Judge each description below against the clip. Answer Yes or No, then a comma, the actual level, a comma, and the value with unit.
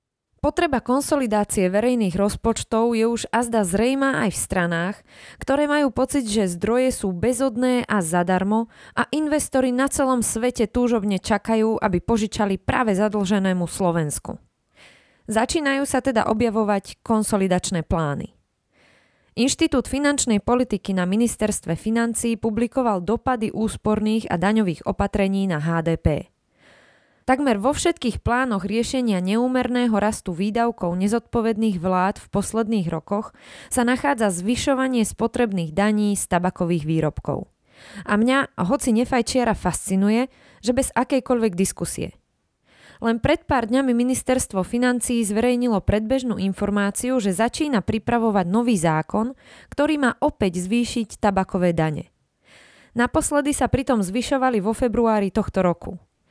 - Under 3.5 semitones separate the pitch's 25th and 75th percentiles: No, average, 3.9 semitones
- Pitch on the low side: No, high, 225 Hz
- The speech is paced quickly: No, average, 115 wpm